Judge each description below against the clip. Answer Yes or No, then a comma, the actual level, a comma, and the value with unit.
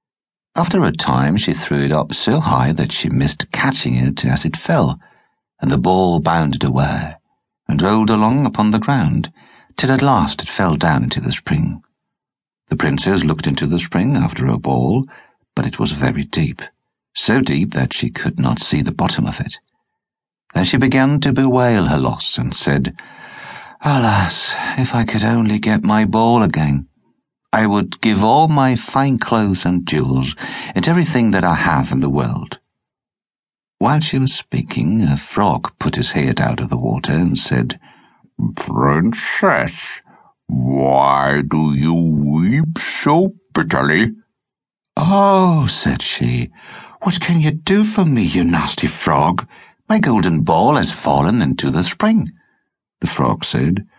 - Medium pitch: No, low, 110 Hz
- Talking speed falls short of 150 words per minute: No, average, 160 wpm